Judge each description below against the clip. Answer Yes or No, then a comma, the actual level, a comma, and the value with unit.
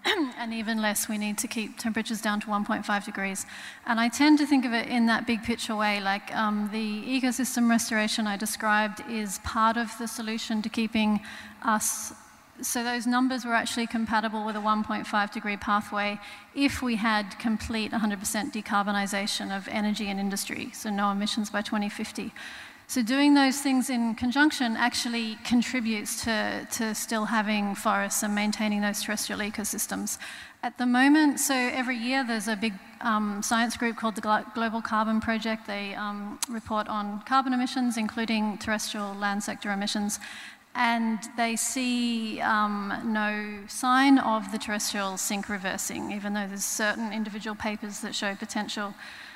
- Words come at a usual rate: Yes, average, 160 wpm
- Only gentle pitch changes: Yes, narrow, 2.2 semitones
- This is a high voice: Yes, high, 220 Hz